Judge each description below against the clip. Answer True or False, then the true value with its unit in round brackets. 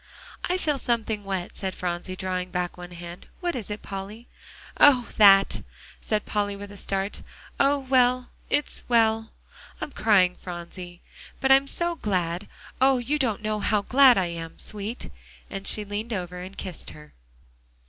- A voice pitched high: True (205 Hz)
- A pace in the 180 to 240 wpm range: False (160 wpm)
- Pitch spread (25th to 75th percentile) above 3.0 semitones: True (5.0 semitones)